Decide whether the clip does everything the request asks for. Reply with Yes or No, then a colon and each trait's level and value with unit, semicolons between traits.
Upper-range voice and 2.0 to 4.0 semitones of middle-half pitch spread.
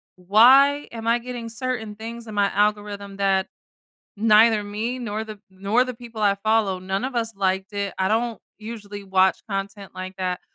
Yes: high, 210 Hz; average, 2.7 semitones